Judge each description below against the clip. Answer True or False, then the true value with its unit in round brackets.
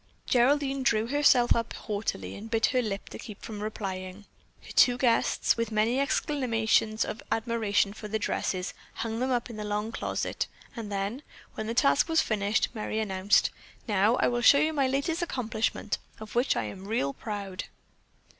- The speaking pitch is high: True (225 Hz)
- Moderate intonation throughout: True (3.2 semitones)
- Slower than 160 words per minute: False (175 wpm)